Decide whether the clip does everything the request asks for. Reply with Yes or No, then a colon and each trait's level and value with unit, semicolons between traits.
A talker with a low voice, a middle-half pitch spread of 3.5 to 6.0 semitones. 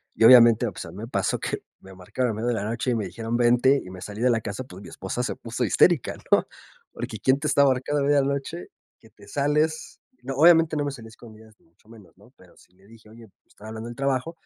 Yes: low, 120 Hz; average, 4.0 semitones